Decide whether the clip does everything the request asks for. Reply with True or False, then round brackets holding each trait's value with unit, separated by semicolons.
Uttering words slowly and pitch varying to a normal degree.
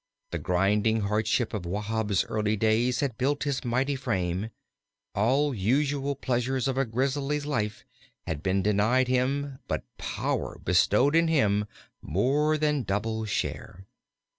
True (130 wpm; 4.8 semitones)